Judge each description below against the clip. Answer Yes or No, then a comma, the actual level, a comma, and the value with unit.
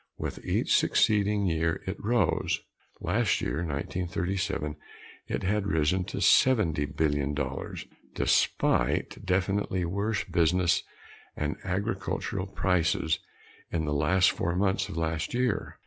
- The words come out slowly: Yes, slow, 115 wpm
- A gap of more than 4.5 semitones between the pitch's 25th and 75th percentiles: No, average, 3.7 semitones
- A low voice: Yes, very low, 90 Hz